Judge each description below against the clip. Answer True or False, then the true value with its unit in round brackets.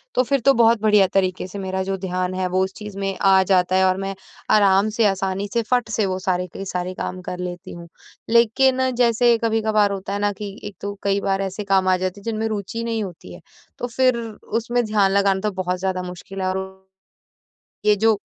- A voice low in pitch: False (195 Hz)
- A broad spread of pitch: False (2.7 semitones)